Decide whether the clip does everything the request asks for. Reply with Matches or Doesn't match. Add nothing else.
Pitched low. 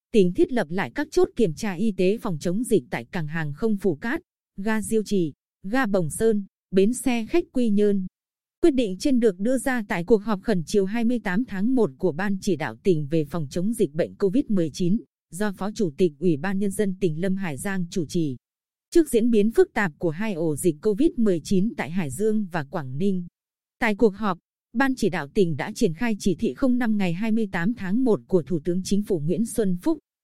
Doesn't match